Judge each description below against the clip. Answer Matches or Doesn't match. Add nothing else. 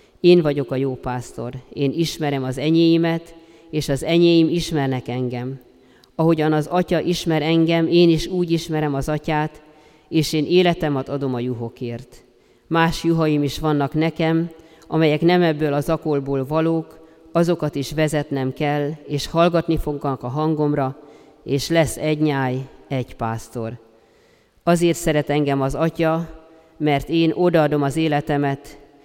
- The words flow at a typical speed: Matches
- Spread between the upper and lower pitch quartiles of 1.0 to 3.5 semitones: Matches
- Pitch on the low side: Doesn't match